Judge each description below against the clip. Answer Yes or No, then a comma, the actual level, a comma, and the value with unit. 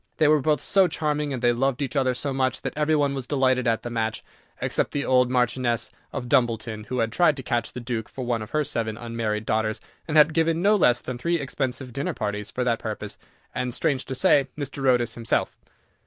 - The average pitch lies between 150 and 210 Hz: No, low, 125 Hz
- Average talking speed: No, fast, 225 wpm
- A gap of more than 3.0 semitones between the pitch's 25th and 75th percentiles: Yes, average, 3.5 semitones